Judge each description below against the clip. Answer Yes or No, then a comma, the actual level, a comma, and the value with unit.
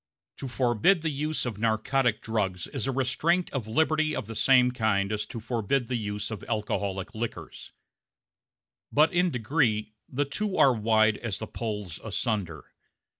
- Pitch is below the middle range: Yes, low, 115 Hz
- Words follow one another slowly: No, average, 160 wpm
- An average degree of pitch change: Yes, average, 4.2 semitones